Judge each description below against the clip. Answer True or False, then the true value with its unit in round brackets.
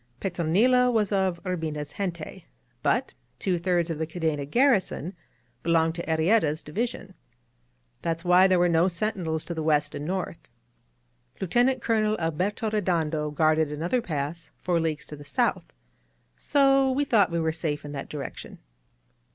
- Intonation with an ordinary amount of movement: True (4.5 semitones)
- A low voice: False (170 Hz)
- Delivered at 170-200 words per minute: False (150 wpm)